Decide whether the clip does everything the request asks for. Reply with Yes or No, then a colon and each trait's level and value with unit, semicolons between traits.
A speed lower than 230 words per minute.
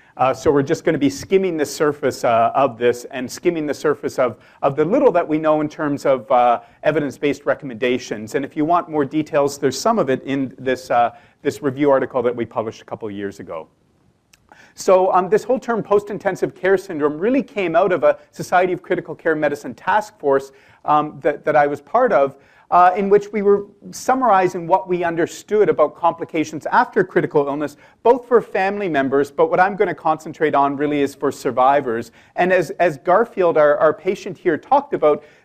Yes: fast, 205 wpm